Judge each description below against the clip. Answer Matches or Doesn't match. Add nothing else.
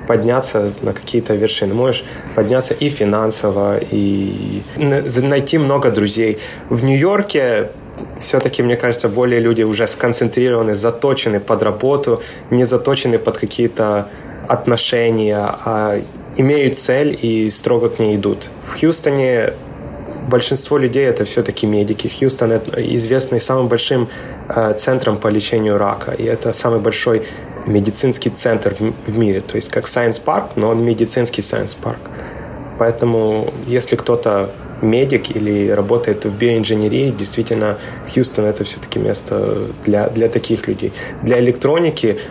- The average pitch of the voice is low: Matches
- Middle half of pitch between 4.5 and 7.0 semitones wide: Doesn't match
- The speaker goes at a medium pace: Matches